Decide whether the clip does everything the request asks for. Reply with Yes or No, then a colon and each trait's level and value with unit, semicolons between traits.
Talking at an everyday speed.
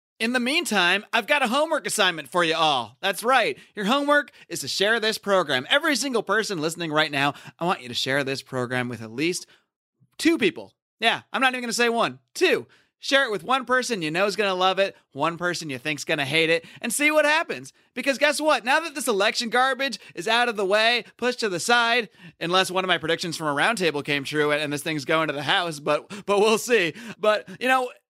No: fast, 235 wpm